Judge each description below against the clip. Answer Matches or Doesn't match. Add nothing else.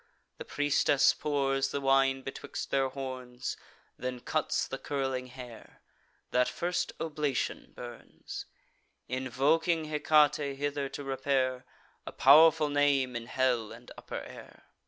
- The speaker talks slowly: Matches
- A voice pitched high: Doesn't match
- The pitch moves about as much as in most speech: Doesn't match